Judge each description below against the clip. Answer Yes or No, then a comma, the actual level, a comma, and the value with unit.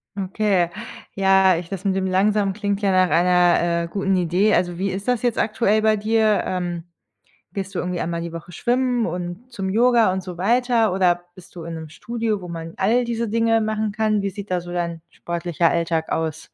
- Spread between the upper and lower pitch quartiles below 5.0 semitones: Yes, average, 3.6 semitones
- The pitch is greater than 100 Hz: Yes, high, 190 Hz